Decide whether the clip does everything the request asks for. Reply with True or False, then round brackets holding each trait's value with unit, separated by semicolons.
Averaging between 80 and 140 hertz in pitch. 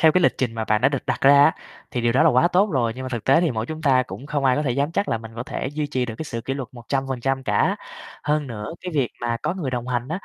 True (135 Hz)